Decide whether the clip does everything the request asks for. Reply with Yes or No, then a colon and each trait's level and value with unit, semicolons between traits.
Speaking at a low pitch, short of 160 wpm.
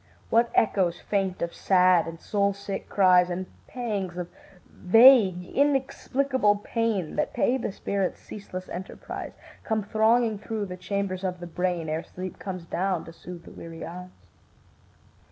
No: high, 190 Hz; average, 150 wpm